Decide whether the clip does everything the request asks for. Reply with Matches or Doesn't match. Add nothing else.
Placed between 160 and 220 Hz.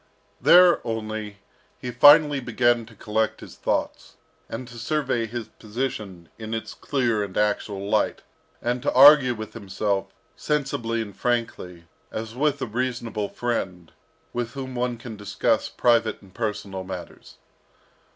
Doesn't match